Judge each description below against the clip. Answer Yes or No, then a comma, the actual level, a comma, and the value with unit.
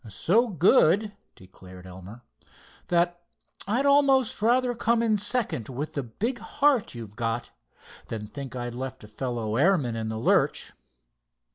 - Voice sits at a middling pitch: Yes, medium, 145 Hz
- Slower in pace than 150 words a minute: Yes, average, 140 wpm